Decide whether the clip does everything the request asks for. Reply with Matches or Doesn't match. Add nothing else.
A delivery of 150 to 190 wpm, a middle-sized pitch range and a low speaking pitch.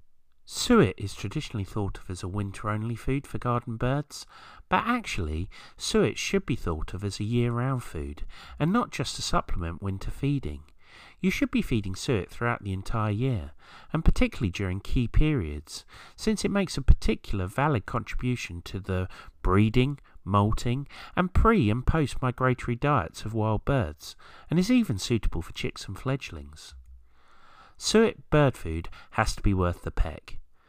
Doesn't match